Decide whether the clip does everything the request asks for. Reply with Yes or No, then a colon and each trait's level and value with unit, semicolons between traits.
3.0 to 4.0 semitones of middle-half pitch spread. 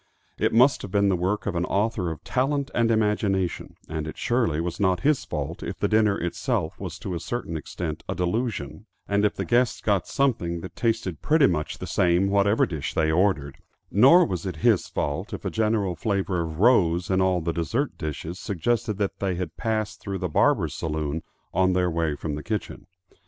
No: average, 4.6 semitones